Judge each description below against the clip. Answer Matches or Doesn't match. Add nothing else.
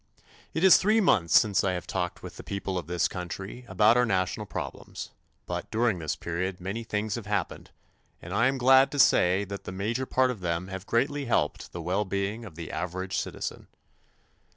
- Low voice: Matches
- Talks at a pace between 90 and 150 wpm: Doesn't match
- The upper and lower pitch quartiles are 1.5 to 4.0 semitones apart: Doesn't match